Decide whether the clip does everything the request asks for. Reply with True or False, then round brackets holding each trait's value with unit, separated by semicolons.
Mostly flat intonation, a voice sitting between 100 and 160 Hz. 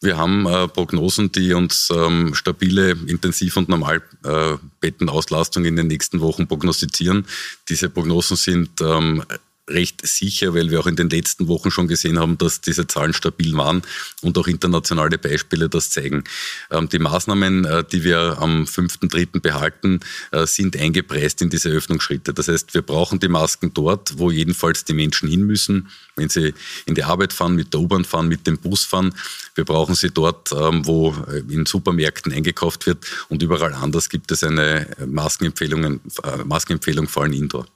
False (2.2 semitones; 85 Hz)